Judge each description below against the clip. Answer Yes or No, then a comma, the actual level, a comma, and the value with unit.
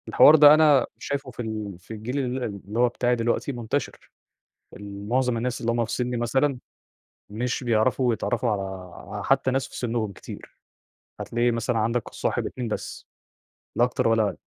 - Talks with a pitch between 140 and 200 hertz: No, low, 120 Hz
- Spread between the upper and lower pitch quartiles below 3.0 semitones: Yes, narrow, 2.5 semitones